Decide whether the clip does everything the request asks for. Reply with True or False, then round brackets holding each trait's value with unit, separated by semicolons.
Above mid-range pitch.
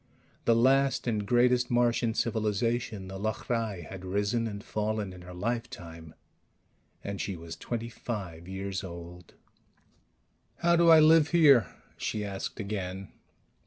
False (105 Hz)